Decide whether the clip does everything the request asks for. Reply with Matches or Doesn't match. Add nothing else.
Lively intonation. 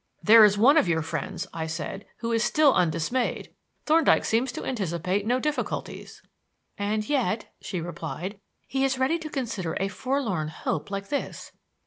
Matches